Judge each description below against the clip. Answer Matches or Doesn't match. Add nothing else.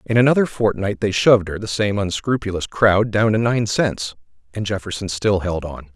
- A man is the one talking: Matches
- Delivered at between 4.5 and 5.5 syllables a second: Matches